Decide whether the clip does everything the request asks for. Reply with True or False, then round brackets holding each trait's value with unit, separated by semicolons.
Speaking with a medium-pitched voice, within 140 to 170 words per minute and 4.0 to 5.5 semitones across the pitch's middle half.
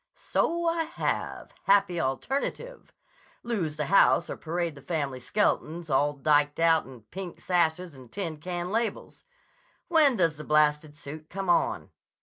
True (165 Hz; 145 wpm; 4.8 semitones)